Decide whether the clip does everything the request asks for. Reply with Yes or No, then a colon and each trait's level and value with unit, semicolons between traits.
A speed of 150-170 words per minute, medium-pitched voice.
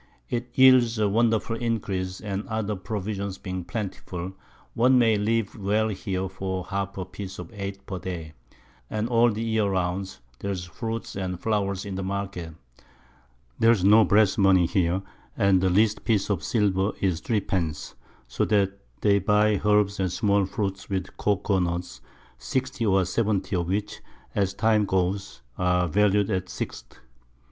No: average, 160 wpm; low, 100 Hz